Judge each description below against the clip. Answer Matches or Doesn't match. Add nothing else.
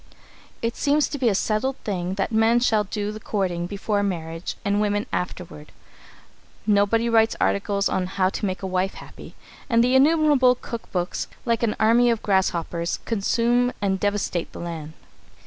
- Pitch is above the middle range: Matches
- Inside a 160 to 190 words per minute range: Matches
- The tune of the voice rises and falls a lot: Doesn't match